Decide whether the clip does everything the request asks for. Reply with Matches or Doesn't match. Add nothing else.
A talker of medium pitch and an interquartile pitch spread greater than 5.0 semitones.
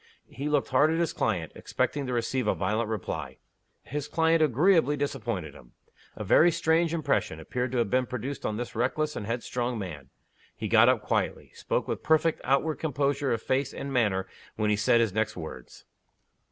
Doesn't match